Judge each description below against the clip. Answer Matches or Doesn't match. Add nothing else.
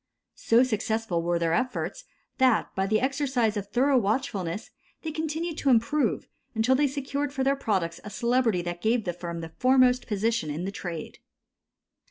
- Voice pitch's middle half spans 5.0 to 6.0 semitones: Matches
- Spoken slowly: Doesn't match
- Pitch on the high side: Matches